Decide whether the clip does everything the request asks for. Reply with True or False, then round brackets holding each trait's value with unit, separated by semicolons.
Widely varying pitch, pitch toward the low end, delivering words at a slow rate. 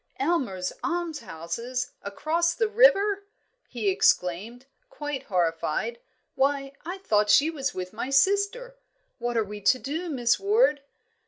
False (8.5 semitones; 275 Hz; 130 wpm)